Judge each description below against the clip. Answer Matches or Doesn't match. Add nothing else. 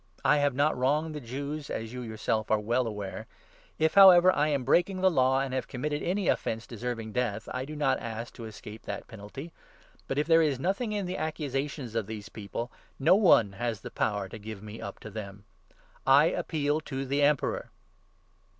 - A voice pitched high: Doesn't match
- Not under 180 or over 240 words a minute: Matches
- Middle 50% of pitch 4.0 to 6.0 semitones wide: Matches